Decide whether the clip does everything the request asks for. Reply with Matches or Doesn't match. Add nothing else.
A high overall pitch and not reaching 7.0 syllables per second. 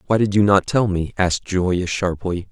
Doesn't match